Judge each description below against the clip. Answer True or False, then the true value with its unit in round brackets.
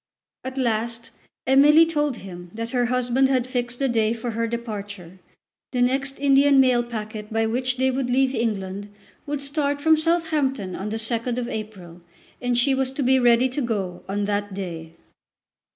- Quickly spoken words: False (175 wpm)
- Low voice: False (240 Hz)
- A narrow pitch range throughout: False (3.7 semitones)